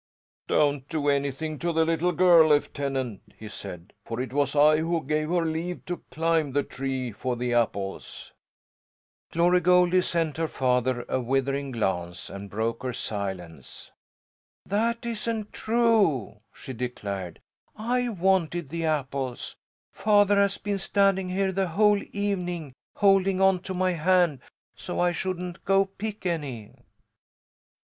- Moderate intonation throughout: No, wide, 6.2 semitones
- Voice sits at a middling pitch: Yes, medium, 160 Hz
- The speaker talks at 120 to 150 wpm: Yes, average, 140 wpm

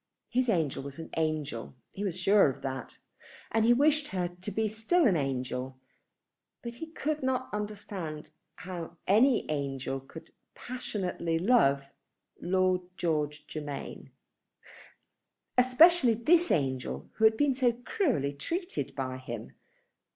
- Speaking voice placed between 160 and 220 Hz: Yes, medium, 185 Hz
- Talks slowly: Yes, slow, 130 wpm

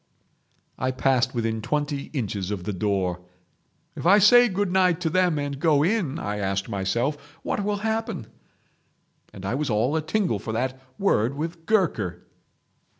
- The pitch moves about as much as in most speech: No, wide, 8.7 semitones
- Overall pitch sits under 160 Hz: Yes, medium, 140 Hz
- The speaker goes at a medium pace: Yes, average, 160 wpm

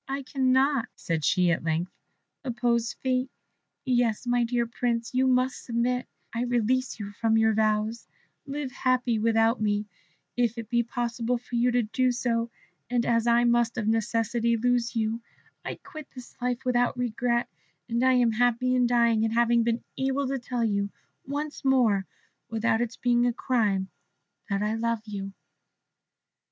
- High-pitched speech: Yes, high, 235 Hz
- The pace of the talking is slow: No, average, 165 wpm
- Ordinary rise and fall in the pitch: No, narrow, 1.8 semitones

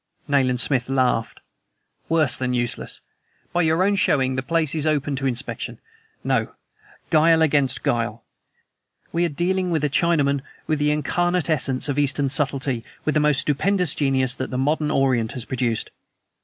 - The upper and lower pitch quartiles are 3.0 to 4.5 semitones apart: Yes, average, 3.5 semitones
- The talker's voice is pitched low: No, medium, 145 Hz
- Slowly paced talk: No, average, 160 wpm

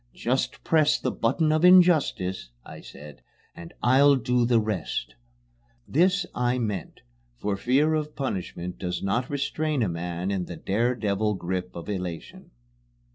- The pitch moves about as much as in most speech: No, wide, 7.5 semitones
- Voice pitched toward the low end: Yes, low, 115 Hz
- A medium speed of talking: Yes, average, 145 wpm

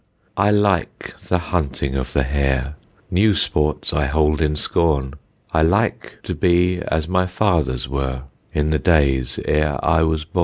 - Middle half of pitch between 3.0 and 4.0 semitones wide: No, average, 4.4 semitones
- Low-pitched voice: Yes, very low, 75 Hz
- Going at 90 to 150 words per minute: No, average, 160 wpm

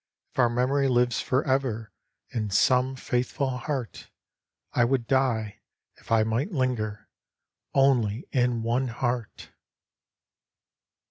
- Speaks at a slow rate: Yes, slow, 120 wpm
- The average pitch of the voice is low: Yes, low, 125 Hz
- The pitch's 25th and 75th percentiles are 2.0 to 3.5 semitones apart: Yes, narrow, 2.5 semitones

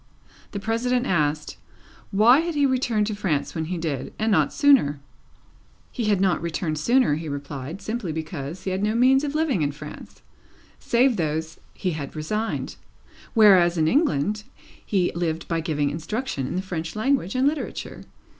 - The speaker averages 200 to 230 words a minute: No, average, 165 wpm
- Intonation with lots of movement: Yes, wide, 6.9 semitones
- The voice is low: No, medium, 185 Hz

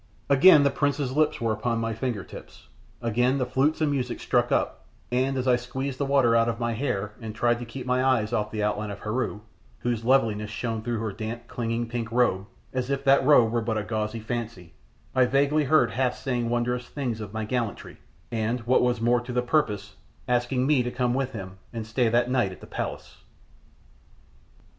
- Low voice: Yes, low, 120 Hz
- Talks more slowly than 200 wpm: No, fast, 205 wpm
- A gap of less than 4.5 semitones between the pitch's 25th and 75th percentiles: Yes, average, 2.7 semitones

